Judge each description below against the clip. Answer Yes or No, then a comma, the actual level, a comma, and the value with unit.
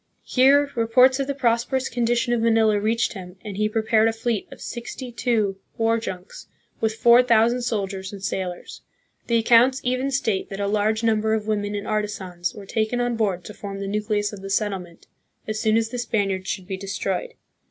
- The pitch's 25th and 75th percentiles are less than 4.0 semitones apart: Yes, average, 2.9 semitones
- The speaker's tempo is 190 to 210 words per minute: Yes, average, 195 wpm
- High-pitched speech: Yes, high, 220 Hz